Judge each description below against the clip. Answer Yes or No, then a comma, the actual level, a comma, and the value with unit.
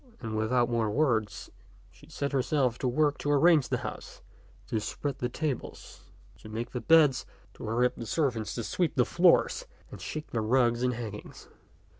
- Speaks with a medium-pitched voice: No, low, 125 Hz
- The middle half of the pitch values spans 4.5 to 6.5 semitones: No, average, 4.1 semitones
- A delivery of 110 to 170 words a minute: No, average, 180 wpm